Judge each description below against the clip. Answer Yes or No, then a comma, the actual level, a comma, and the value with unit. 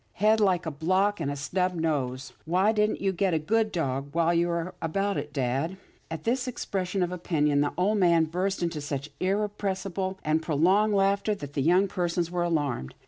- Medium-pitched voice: Yes, medium, 175 Hz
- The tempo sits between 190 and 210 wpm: Yes, average, 195 wpm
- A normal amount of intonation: Yes, average, 4.2 semitones